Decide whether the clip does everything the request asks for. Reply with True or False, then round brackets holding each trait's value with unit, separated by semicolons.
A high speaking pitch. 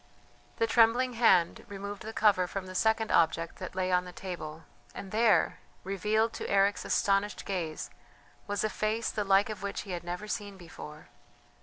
True (200 Hz)